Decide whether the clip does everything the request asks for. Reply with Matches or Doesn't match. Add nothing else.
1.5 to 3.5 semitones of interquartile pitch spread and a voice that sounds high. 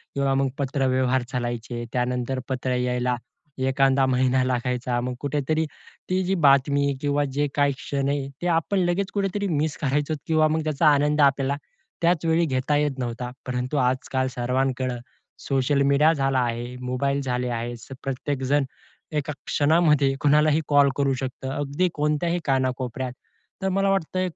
Doesn't match